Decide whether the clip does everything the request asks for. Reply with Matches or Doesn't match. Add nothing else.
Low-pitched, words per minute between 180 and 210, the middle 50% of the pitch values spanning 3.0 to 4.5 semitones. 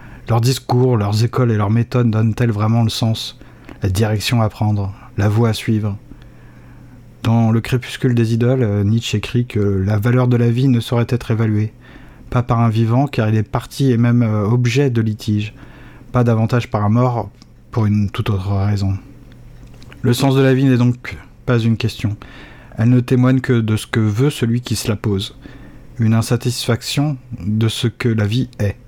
Doesn't match